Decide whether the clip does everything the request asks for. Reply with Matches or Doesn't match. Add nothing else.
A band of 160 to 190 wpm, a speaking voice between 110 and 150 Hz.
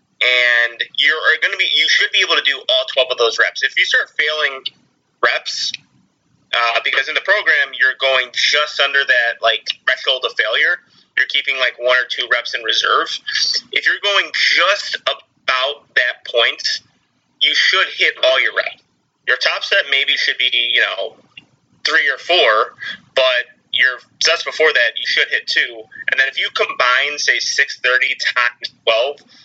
Matches